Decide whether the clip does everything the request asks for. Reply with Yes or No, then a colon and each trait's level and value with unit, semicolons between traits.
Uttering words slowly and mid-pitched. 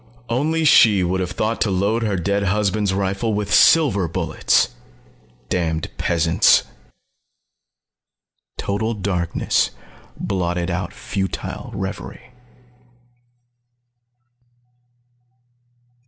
No: slow, 85 wpm; low, 100 Hz